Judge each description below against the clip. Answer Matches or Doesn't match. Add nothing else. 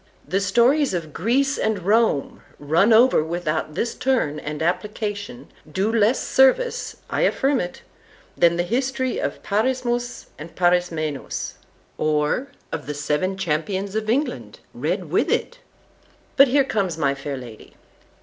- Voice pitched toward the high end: Matches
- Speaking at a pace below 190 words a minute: Matches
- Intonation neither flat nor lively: Doesn't match